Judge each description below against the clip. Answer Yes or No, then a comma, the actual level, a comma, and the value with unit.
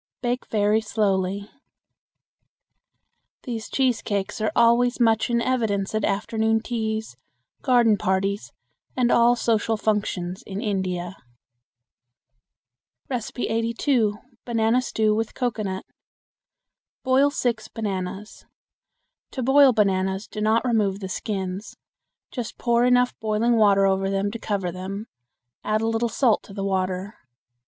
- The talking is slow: Yes, slow, 120 wpm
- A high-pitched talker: Yes, high, 220 Hz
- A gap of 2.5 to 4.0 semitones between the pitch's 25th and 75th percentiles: Yes, average, 3.1 semitones